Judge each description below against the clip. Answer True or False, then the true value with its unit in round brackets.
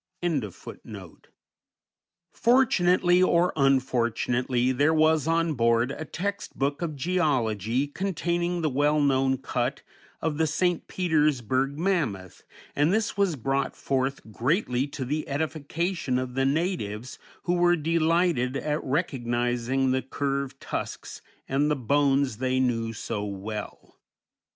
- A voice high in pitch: False (140 Hz)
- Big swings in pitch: False (4.7 semitones)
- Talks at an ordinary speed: False (120 wpm)